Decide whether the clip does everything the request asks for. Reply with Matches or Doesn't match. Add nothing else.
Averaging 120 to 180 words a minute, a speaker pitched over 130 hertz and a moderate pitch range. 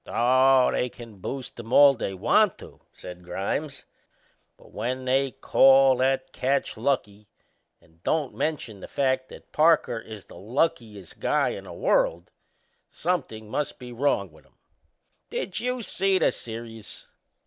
Doesn't match